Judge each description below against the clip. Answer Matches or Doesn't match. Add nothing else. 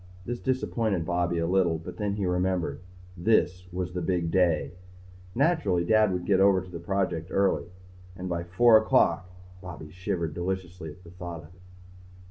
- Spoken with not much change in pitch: Matches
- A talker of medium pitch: Doesn't match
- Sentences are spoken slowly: Doesn't match